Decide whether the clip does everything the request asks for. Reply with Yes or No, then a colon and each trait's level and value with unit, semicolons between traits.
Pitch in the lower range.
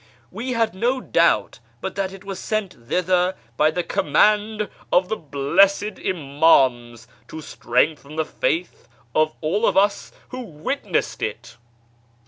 No: medium, 180 Hz